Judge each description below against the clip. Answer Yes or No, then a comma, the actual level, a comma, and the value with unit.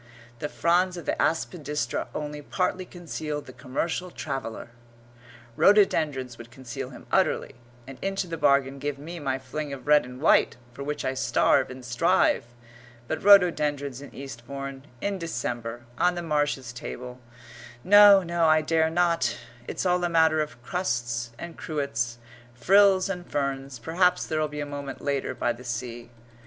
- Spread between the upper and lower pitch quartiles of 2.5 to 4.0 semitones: No, average, 4.8 semitones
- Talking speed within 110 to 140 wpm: No, average, 160 wpm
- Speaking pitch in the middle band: Yes, medium, 145 Hz